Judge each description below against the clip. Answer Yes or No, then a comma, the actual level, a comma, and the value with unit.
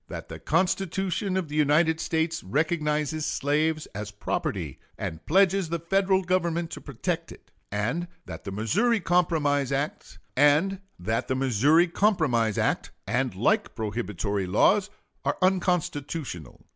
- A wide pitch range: Yes, wide, 6.2 semitones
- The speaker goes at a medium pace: No, slow, 110 wpm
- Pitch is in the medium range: Yes, medium, 155 Hz